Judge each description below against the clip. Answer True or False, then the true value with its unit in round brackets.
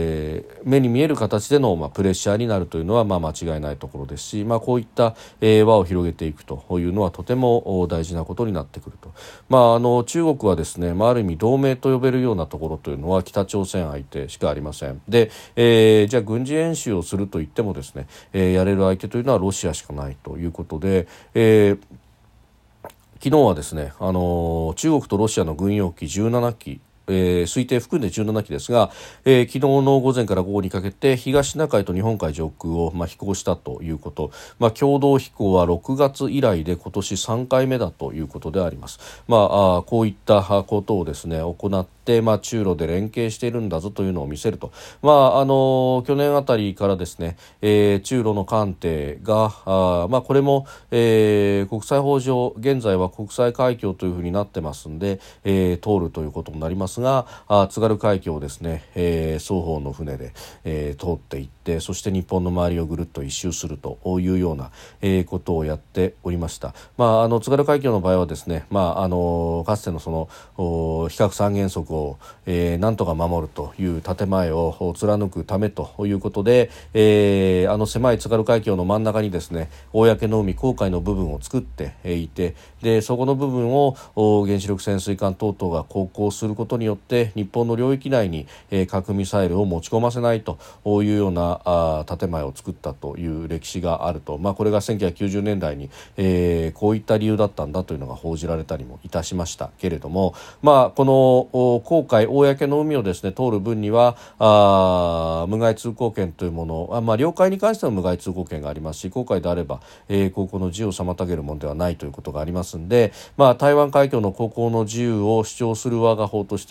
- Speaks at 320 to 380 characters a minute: True (355 characters per minute)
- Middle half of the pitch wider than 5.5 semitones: False (5.1 semitones)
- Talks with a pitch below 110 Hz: True (100 Hz)